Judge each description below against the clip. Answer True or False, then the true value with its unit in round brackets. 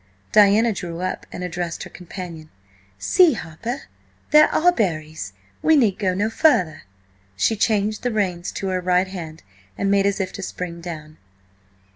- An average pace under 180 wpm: True (155 wpm)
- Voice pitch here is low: False (185 Hz)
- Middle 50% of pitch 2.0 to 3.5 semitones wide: False (4.0 semitones)